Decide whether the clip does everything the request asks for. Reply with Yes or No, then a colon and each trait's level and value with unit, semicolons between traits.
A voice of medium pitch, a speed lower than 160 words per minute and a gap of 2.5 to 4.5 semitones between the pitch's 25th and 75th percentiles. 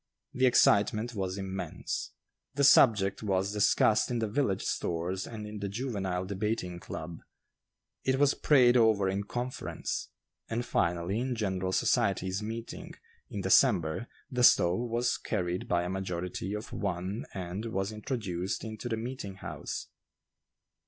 No: low, 100 Hz; average, 140 wpm; average, 3.7 semitones